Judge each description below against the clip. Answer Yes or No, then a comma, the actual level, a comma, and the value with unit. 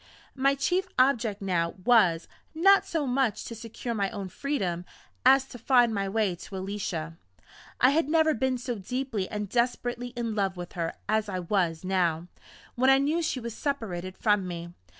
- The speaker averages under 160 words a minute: No, average, 175 wpm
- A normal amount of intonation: No, wide, 5.9 semitones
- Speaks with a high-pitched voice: Yes, high, 225 Hz